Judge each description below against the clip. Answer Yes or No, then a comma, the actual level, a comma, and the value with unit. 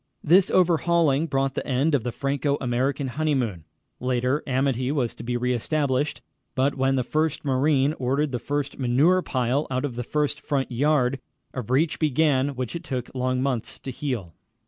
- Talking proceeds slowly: No, average, 175 wpm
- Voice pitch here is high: No, low, 135 Hz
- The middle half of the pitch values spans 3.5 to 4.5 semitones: No, average, 2.7 semitones